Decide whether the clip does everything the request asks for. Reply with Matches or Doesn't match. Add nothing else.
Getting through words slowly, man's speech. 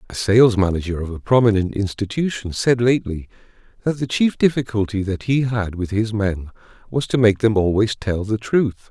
Doesn't match